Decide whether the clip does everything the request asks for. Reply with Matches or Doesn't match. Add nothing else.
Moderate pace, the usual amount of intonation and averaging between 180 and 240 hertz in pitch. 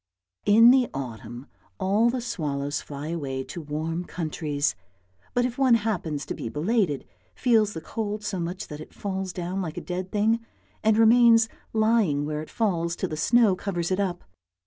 Doesn't match